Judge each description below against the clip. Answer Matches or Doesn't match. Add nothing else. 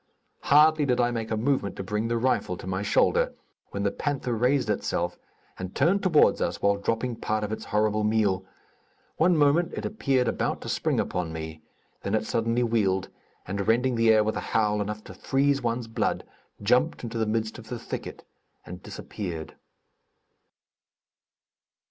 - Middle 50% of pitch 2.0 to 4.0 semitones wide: Matches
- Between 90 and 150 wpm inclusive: Doesn't match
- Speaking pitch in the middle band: Doesn't match